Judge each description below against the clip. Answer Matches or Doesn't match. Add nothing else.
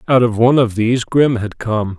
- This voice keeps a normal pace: Doesn't match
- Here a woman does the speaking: Doesn't match